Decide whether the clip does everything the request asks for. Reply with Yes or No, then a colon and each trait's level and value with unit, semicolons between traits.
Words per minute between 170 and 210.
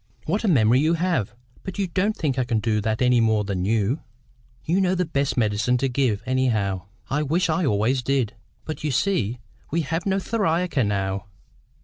Yes: average, 200 wpm